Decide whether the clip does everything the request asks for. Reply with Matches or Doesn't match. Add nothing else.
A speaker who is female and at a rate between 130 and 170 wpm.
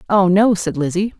Doesn't match